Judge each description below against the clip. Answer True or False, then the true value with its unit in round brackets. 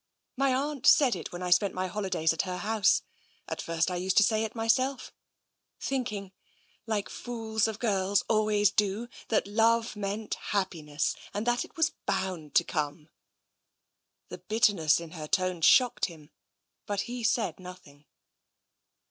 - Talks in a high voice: True (205 Hz)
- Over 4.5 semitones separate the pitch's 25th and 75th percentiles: False (4.0 semitones)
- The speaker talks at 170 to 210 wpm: False (155 wpm)